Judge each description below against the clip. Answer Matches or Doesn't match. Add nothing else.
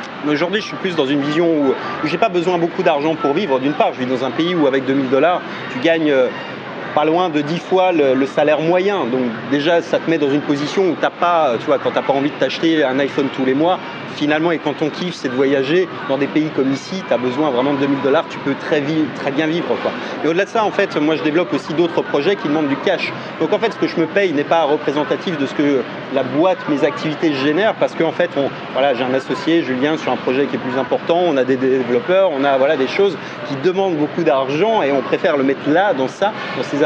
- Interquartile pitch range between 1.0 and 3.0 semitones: Doesn't match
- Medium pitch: Matches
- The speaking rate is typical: Doesn't match